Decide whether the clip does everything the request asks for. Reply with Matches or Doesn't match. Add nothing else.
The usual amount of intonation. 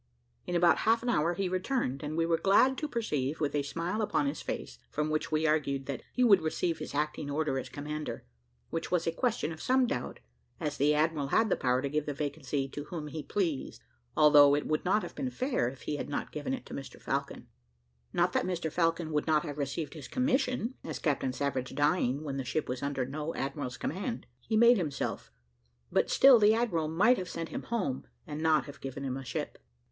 Matches